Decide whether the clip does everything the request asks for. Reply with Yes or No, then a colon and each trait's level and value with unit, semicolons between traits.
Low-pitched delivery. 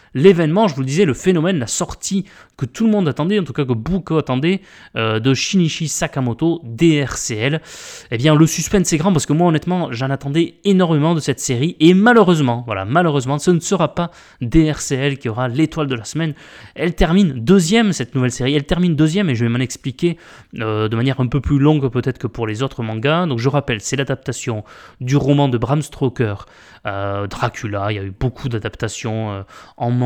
No: medium, 145 Hz